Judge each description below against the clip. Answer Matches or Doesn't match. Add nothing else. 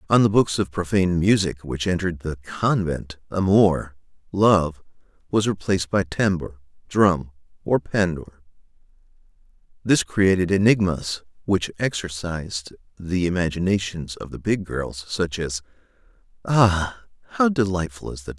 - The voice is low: Matches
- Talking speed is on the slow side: Matches